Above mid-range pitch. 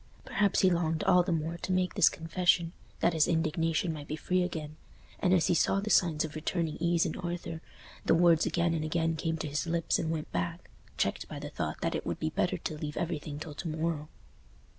No: medium, 165 Hz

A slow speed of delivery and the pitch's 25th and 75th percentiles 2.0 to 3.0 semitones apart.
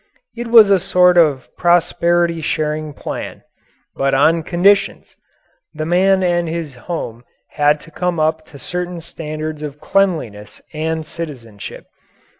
Yes: slow, 130 wpm; narrow, 2.6 semitones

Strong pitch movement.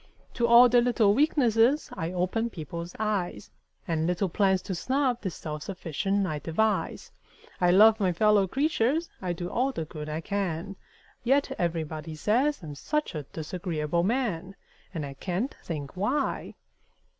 Yes: wide, 6.1 semitones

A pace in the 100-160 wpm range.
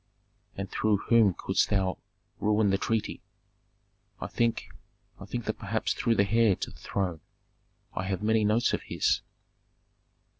Yes: average, 150 wpm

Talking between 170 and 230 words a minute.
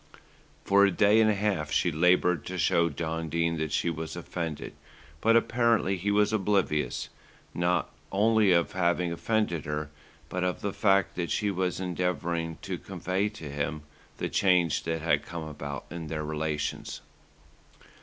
No: average, 160 wpm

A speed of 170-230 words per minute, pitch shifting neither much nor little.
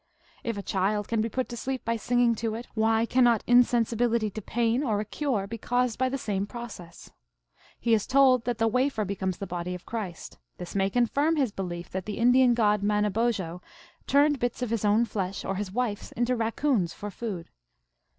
Yes: average, 200 wpm; average, 3.2 semitones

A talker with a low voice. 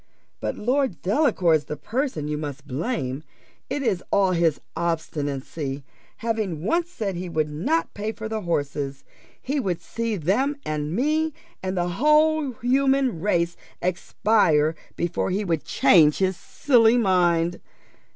No: medium, 185 Hz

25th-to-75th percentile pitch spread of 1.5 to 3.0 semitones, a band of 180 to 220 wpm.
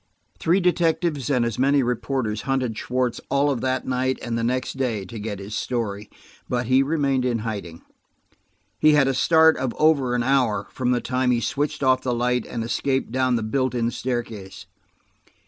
Yes: narrow, 2.6 semitones; average, 185 wpm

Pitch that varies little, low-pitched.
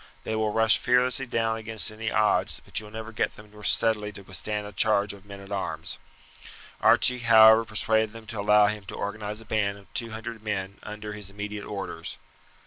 Yes: narrow, 1.5 semitones; low, 105 Hz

